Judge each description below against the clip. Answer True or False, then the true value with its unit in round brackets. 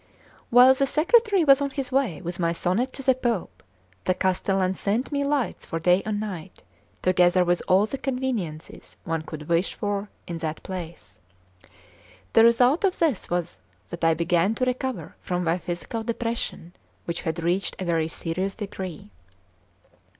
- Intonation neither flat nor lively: False (6.7 semitones)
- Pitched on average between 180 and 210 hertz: True (190 Hz)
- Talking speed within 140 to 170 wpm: True (165 wpm)